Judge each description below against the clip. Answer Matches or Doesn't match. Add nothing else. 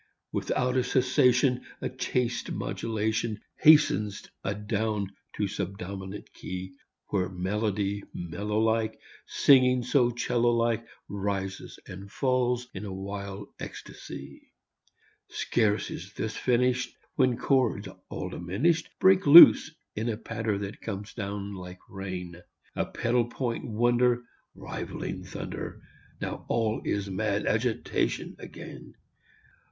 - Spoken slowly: Matches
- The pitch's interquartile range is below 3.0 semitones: Doesn't match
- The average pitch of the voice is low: Matches